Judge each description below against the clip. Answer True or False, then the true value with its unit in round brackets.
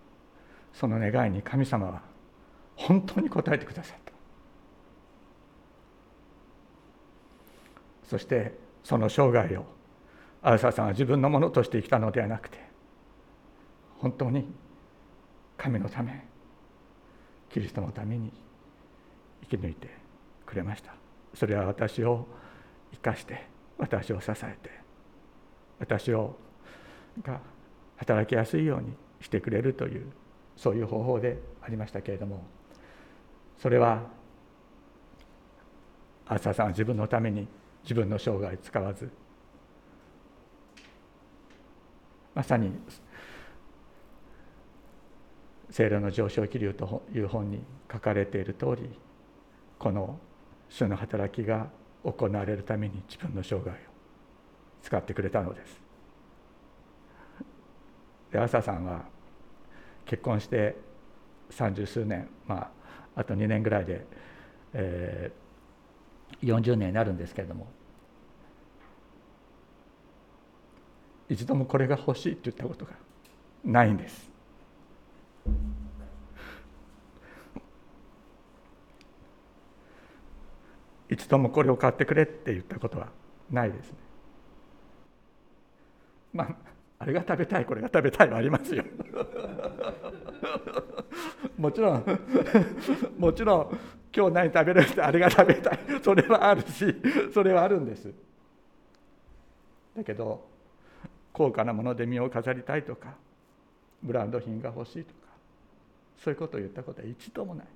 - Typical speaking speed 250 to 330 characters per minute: False (215 characters per minute)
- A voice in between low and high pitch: False (115 Hz)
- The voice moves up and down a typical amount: True (4.6 semitones)